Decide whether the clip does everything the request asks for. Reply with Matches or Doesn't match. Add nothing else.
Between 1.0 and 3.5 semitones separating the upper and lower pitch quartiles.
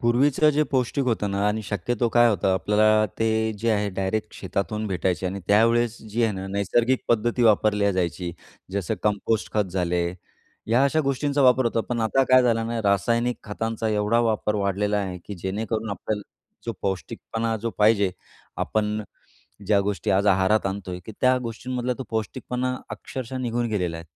Matches